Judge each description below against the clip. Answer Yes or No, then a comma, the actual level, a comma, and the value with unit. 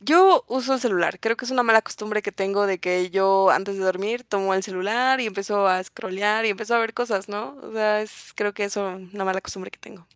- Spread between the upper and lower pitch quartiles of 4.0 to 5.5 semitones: No, average, 2.8 semitones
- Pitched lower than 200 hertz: No, high, 205 Hz